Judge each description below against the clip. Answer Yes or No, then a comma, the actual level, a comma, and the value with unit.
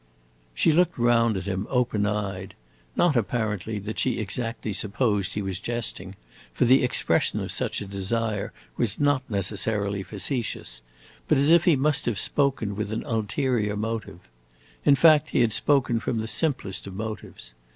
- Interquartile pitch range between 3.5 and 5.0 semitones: Yes, average, 3.9 semitones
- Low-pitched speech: Yes, low, 110 Hz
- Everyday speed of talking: Yes, average, 160 wpm